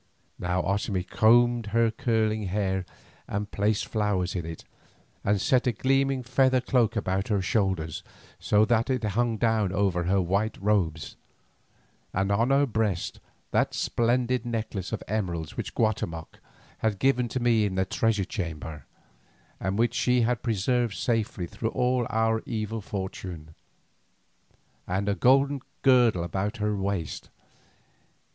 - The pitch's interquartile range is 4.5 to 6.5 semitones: No, average, 3.8 semitones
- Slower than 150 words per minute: Yes, average, 140 wpm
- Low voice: Yes, low, 105 Hz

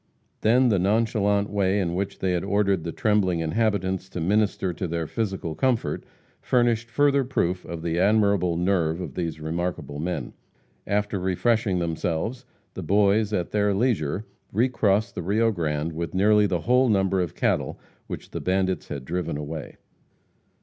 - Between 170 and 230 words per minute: No, average, 155 wpm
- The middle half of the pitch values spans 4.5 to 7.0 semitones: No, average, 3.8 semitones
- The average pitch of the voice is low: Yes, very low, 95 Hz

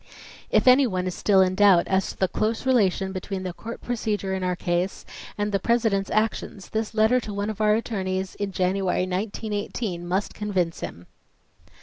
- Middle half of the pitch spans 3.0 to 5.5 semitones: No, narrow, 2.6 semitones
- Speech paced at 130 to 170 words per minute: No, average, 185 wpm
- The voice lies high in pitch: Yes, high, 195 Hz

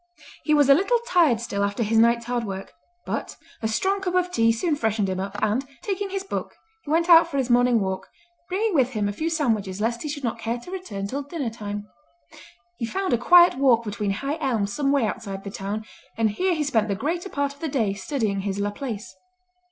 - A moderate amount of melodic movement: No, wide, 6.8 semitones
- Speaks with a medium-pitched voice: No, high, 240 Hz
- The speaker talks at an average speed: No, fast, 225 wpm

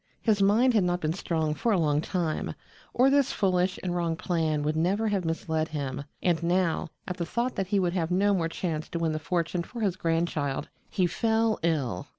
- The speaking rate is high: Yes, fast, 210 wpm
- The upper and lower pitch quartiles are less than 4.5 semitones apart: Yes, average, 3.5 semitones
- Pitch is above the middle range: No, medium, 175 Hz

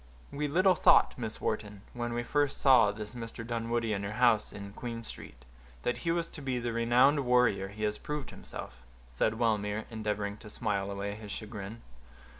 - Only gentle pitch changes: No, average, 3.0 semitones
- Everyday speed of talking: Yes, average, 185 wpm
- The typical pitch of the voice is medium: No, low, 115 Hz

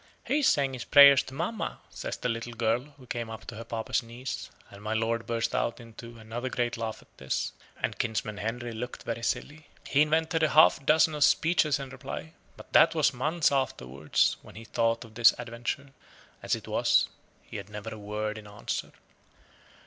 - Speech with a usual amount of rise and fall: Yes, average, 3.8 semitones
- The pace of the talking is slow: No, average, 195 wpm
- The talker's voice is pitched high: No, low, 120 Hz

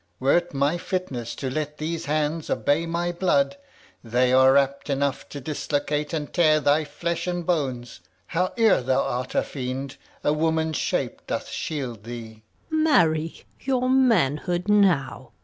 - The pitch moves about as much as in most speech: Yes, average, 3.9 semitones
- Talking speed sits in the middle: No, slow, 130 wpm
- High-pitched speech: No, medium, 150 Hz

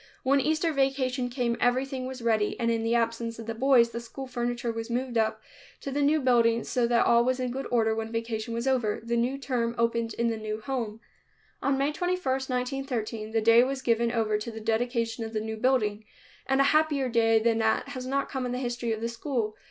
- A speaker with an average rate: No, fast, 225 wpm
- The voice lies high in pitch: Yes, high, 235 Hz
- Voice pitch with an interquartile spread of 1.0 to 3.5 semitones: Yes, narrow, 2.5 semitones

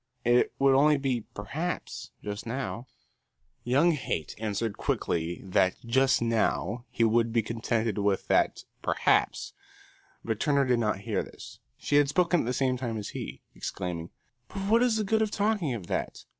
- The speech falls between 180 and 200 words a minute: No, average, 170 wpm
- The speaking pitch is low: Yes, low, 120 Hz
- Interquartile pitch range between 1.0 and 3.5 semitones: No, average, 5.1 semitones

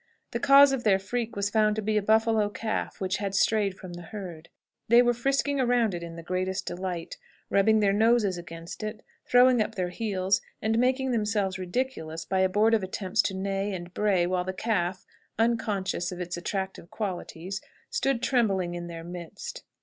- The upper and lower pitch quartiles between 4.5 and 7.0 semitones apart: No, average, 3.6 semitones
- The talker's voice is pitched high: Yes, high, 200 Hz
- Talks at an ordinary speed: Yes, average, 180 wpm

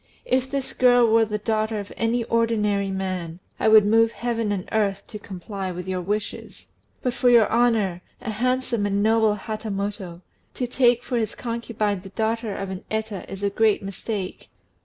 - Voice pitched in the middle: No, high, 215 Hz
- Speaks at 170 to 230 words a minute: Yes, average, 180 wpm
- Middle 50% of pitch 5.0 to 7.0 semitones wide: No, narrow, 2.6 semitones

